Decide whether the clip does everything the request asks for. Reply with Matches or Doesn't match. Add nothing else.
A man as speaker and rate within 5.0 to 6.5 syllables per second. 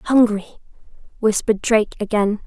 Doesn't match